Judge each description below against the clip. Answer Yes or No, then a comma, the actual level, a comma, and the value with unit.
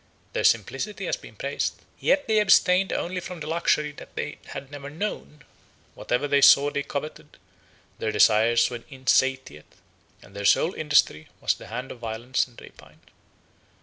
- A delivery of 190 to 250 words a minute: No, average, 155 wpm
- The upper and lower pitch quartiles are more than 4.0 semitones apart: Yes, average, 4.9 semitones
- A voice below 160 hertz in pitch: Yes, medium, 140 Hz